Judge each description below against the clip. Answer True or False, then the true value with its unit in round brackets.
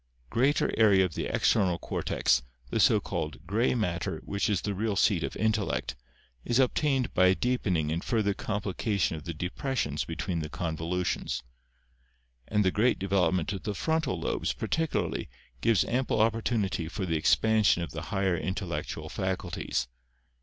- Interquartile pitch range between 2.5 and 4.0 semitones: False (4.4 semitones)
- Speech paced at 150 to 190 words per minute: True (160 wpm)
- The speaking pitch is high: False (100 Hz)